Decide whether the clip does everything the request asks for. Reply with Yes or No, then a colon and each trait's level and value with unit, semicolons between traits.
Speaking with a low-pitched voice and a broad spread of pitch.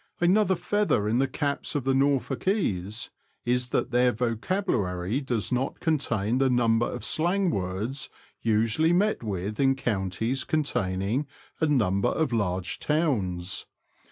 Yes: low, 125 Hz; wide, 6.0 semitones